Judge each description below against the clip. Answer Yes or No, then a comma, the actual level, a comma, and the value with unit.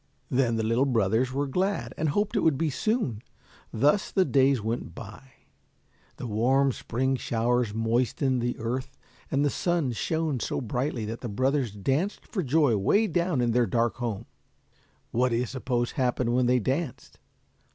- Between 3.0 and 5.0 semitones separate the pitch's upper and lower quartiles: Yes, average, 3.4 semitones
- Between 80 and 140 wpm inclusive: No, average, 170 wpm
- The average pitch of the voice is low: Yes, low, 125 Hz